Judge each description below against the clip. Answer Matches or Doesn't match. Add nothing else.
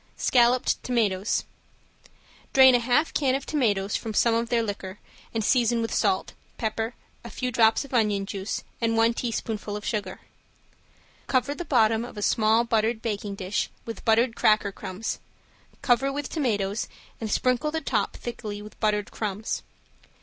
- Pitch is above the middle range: Matches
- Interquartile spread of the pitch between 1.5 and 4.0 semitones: Matches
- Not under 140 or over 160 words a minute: Matches